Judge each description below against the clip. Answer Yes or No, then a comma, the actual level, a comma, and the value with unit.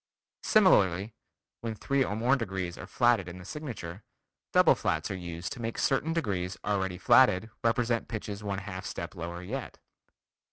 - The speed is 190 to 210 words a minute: No, average, 160 wpm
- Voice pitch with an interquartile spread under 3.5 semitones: No, average, 4.6 semitones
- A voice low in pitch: Yes, low, 100 Hz